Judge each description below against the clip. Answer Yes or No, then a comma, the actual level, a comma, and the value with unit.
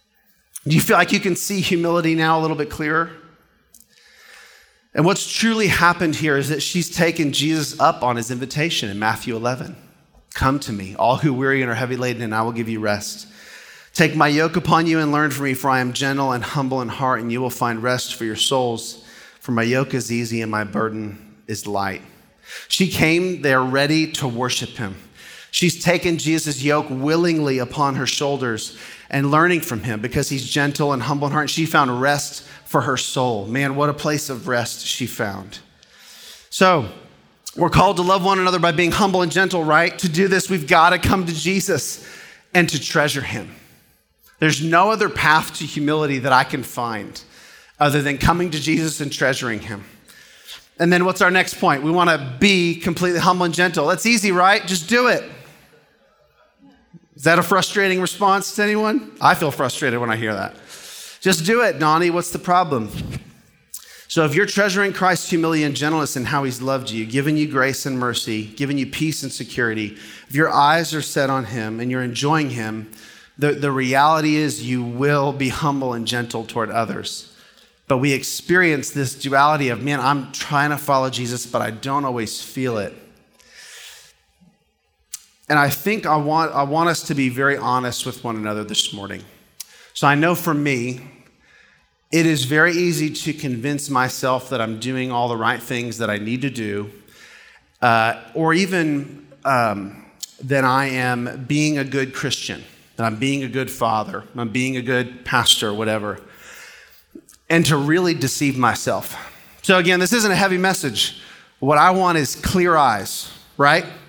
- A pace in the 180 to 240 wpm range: Yes, average, 185 wpm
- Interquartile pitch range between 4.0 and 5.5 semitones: Yes, average, 4.8 semitones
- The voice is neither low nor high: Yes, medium, 145 Hz